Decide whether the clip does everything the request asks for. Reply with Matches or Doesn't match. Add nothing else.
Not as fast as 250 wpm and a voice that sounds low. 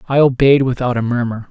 Matches